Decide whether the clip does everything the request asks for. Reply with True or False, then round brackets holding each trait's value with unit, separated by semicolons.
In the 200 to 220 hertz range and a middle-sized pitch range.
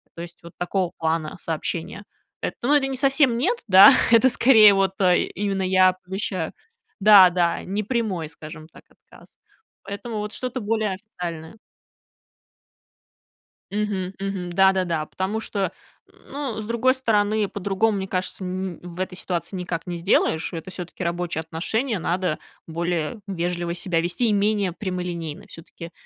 False (190 Hz; 3.5 semitones)